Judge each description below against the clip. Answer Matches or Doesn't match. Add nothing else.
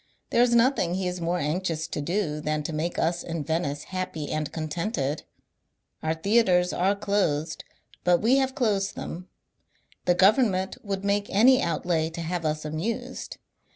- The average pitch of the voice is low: Doesn't match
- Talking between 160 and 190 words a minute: Matches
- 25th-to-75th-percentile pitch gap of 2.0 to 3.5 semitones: Doesn't match